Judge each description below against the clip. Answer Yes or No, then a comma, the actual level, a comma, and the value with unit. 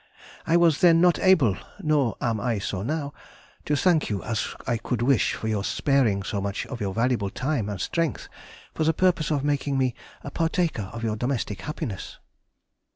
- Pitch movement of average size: No, wide, 6.4 semitones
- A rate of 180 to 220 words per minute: Yes, average, 185 wpm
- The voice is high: No, low, 130 Hz